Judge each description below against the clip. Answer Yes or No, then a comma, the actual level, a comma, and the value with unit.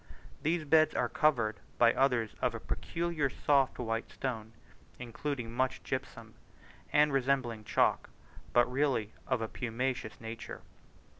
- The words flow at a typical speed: No, slow, 130 wpm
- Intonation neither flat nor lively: Yes, average, 3.5 semitones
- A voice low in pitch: Yes, low, 125 Hz